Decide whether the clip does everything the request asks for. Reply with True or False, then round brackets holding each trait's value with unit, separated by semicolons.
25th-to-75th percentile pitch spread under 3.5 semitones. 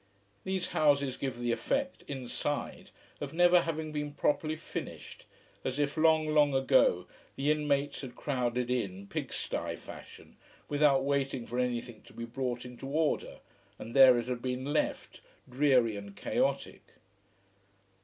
True (3.1 semitones)